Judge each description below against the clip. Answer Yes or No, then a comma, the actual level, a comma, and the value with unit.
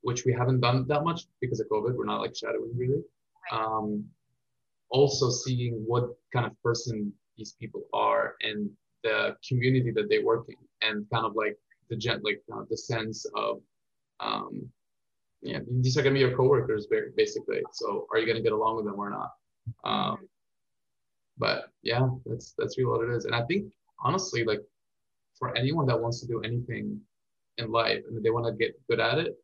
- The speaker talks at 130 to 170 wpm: No, average, 200 wpm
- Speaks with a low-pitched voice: Yes, low, 125 Hz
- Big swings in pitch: Yes, wide, 6.6 semitones